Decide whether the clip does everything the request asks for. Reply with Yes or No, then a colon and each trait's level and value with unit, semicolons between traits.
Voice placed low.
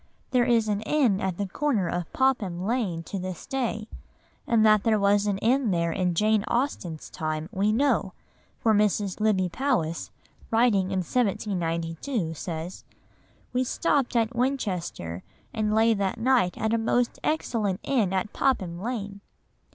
No: high, 210 Hz